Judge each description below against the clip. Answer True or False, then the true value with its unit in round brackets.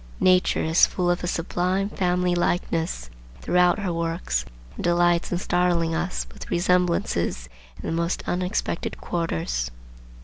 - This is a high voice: False (175 Hz)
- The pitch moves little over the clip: True (1.4 semitones)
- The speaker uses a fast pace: False (135 wpm)